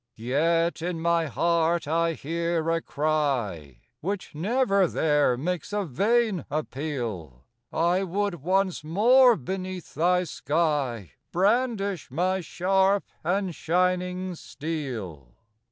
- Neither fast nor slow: No, slow, 105 wpm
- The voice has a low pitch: No, medium, 170 Hz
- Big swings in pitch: No, average, 4.1 semitones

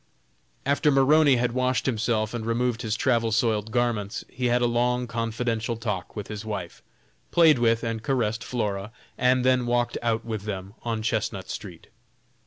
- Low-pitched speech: Yes, low, 115 Hz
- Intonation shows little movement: Yes, narrow, 2.2 semitones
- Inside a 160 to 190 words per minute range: Yes, average, 165 wpm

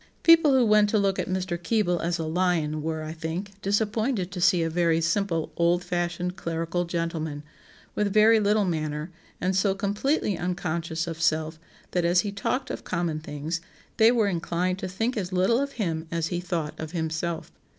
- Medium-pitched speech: Yes, medium, 175 Hz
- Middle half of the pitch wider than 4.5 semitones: No, average, 3.5 semitones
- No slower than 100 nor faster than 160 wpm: No, average, 190 wpm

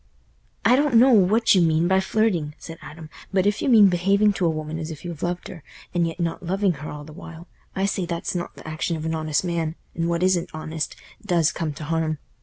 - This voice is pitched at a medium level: Yes, medium, 170 Hz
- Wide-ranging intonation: No, average, 3.1 semitones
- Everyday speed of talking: No, fast, 235 wpm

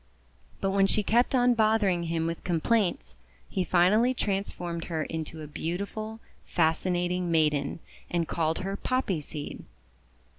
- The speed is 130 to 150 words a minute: Yes, average, 140 wpm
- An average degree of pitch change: Yes, average, 4.2 semitones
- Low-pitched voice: No, medium, 180 Hz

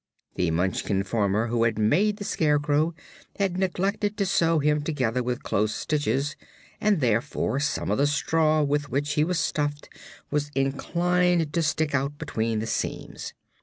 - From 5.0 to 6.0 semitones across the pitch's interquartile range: Yes, average, 5.3 semitones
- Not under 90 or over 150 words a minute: No, average, 160 wpm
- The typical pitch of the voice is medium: Yes, medium, 145 Hz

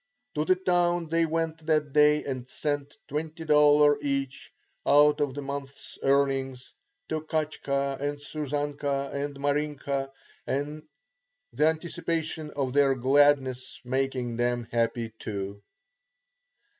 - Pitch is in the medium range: Yes, medium, 145 Hz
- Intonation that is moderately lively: No, narrow, 2.2 semitones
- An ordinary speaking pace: No, slow, 110 wpm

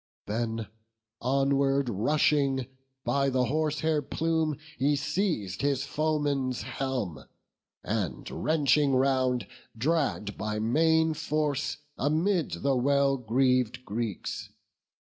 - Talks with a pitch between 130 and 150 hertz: Yes, low, 135 Hz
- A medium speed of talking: No, slow, 95 wpm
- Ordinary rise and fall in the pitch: Yes, average, 3.5 semitones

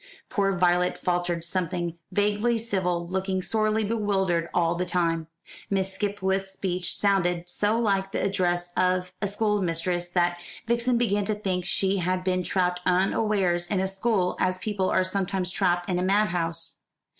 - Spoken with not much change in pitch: Yes, narrow, 2.3 semitones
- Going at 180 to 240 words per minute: No, average, 155 wpm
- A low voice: No, medium, 185 Hz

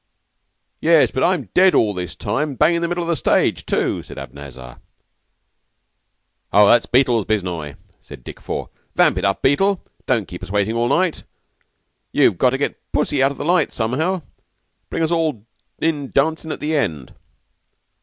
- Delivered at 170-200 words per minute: Yes, average, 175 wpm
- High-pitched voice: No, low, 135 Hz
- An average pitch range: No, wide, 7.9 semitones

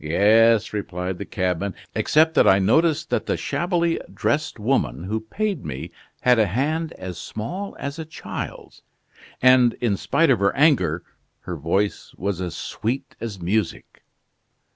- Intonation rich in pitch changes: Yes, wide, 8.1 semitones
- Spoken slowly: No, average, 150 wpm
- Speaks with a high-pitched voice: No, low, 110 Hz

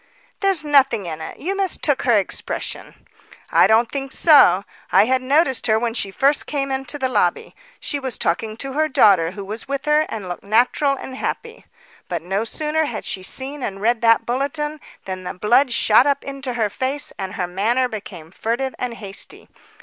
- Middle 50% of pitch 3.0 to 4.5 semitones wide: No, average, 5.2 semitones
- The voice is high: Yes, high, 245 Hz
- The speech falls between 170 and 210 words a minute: Yes, average, 190 wpm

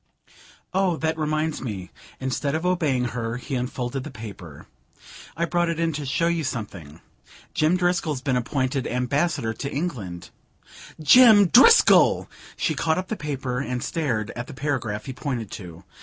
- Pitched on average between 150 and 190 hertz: No, medium, 140 Hz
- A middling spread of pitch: Yes, average, 4.9 semitones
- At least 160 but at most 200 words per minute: Yes, average, 165 wpm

